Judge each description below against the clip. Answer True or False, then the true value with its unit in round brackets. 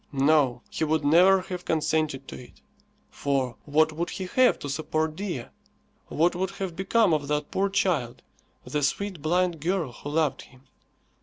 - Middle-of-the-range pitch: True (160 Hz)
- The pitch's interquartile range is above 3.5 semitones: True (4.0 semitones)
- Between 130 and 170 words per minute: True (165 wpm)